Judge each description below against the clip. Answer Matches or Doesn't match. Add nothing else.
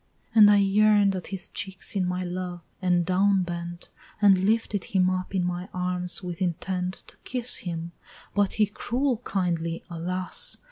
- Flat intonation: Matches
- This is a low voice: Doesn't match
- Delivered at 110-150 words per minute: Doesn't match